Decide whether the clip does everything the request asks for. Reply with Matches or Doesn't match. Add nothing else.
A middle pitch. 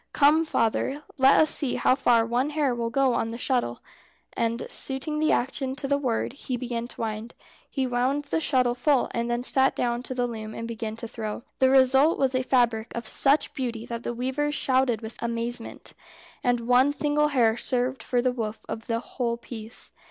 Doesn't match